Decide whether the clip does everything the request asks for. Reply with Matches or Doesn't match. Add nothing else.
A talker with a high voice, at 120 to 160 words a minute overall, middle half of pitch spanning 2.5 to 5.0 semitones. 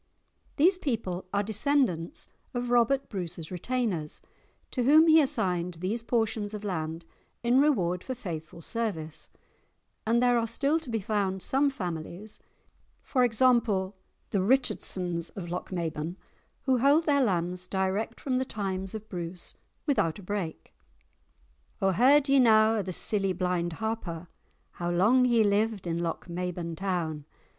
Doesn't match